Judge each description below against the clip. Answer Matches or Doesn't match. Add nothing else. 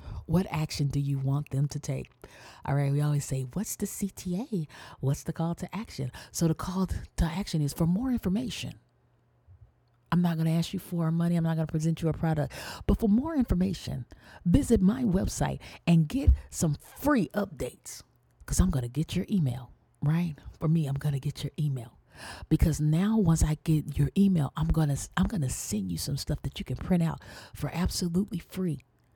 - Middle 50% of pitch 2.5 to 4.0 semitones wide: Doesn't match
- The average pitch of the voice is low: Doesn't match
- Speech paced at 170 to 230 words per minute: Matches